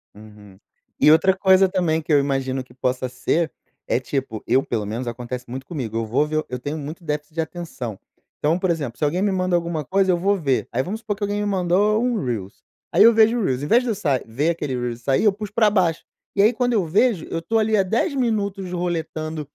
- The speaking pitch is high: No, medium, 165 Hz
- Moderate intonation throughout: No, wide, 7.1 semitones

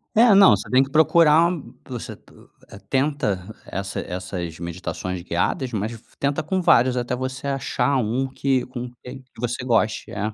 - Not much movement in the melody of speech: No, average, 4.5 semitones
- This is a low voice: Yes, low, 125 Hz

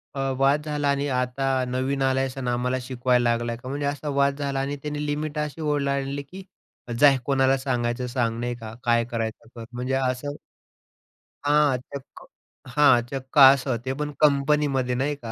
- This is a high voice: No, low, 135 Hz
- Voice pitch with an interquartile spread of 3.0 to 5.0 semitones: No, narrow, 2.4 semitones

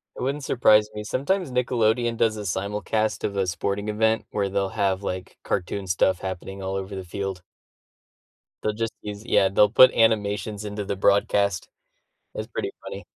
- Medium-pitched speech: No, low, 100 Hz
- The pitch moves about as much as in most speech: No, narrow, 2.3 semitones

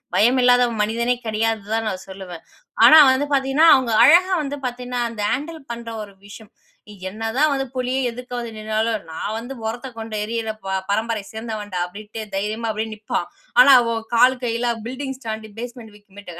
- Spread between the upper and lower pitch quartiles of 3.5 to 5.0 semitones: No, narrow, 2.6 semitones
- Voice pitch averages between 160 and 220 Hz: No, high, 230 Hz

